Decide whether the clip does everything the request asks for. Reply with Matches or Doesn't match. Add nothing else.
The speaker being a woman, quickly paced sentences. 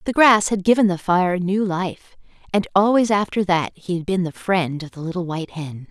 Matches